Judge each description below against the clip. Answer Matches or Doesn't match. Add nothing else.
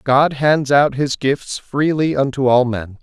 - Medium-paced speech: Matches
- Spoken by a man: Matches